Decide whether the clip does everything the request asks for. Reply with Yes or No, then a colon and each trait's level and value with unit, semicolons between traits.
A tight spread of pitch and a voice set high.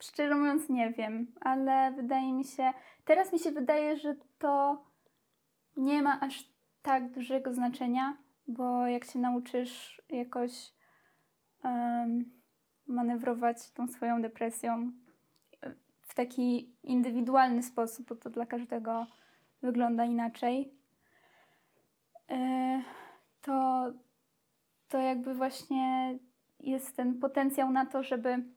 Yes: narrow, 1.7 semitones; very high, 255 Hz